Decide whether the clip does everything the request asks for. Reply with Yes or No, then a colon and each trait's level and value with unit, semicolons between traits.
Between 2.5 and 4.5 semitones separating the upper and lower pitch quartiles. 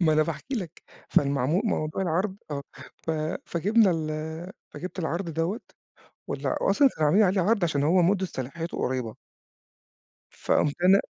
Yes: average, 3.8 semitones